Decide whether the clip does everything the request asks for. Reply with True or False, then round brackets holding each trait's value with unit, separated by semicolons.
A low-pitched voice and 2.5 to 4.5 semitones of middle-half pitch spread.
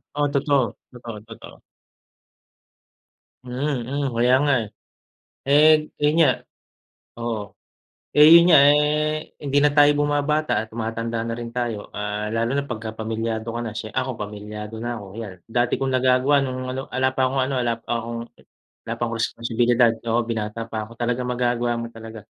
True (120 Hz; 3.3 semitones)